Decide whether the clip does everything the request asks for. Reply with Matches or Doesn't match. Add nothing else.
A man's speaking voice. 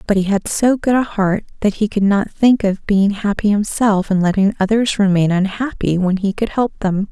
Doesn't match